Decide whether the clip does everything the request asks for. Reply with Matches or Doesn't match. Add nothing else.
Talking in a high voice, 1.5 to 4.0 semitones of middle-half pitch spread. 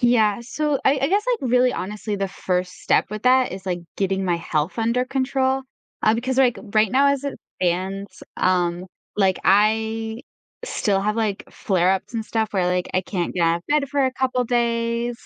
Doesn't match